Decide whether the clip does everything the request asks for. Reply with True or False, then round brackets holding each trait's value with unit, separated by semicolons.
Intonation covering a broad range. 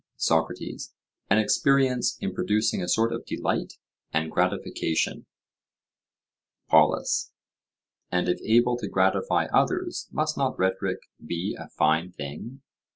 True (7.7 semitones)